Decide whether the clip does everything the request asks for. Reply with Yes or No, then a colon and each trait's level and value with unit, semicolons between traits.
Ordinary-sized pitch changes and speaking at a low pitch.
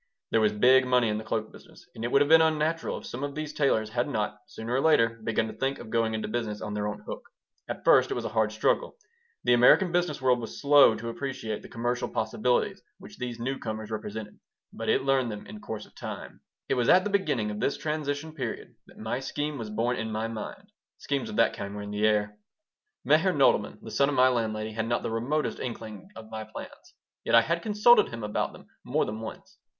Yes: average, 4.4 semitones; low, 115 Hz